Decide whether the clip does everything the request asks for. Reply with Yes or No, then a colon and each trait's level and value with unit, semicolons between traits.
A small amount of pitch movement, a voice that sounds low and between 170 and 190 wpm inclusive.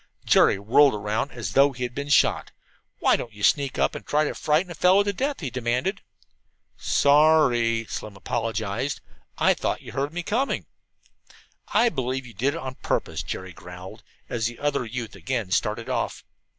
No: average, 4.6 semitones; low, 130 Hz; average, 175 wpm